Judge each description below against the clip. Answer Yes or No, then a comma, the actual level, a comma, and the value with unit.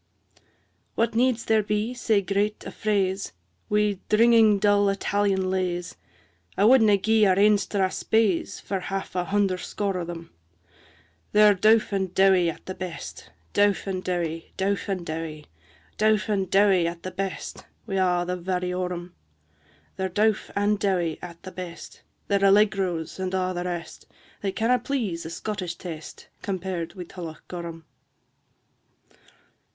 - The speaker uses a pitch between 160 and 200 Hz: Yes, high, 190 Hz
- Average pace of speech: Yes, average, 145 wpm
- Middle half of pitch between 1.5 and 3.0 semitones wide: Yes, narrow, 2.6 semitones